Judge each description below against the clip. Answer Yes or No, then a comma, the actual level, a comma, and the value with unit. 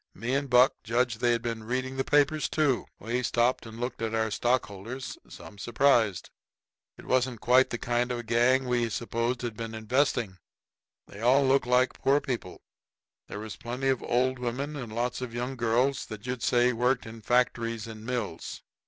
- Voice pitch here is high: No, low, 120 Hz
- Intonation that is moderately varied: No, narrow, 2.0 semitones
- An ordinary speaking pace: Yes, average, 180 wpm